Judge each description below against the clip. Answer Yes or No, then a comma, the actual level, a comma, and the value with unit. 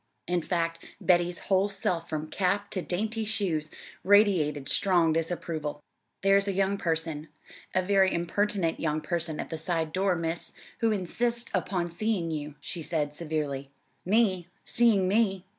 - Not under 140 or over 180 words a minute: Yes, average, 145 wpm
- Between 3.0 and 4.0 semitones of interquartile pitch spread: Yes, average, 3.5 semitones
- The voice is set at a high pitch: No, medium, 175 Hz